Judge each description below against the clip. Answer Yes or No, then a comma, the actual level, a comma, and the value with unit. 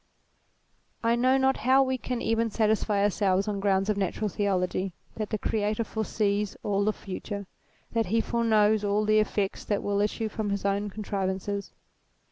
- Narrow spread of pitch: Yes, narrow, 1.8 semitones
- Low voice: No, high, 210 Hz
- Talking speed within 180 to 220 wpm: No, average, 165 wpm